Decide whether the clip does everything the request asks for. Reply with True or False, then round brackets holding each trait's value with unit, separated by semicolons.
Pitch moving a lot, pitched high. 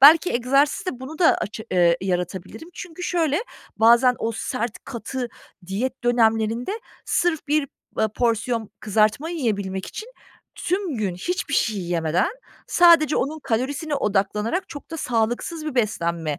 True (6.5 semitones; 240 Hz)